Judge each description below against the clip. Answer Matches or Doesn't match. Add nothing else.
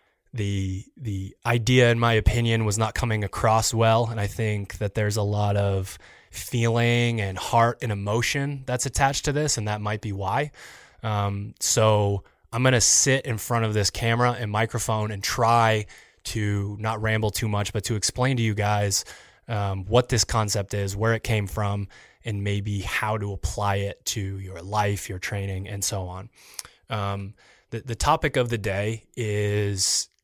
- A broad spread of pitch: Doesn't match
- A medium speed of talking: Matches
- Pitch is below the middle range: Matches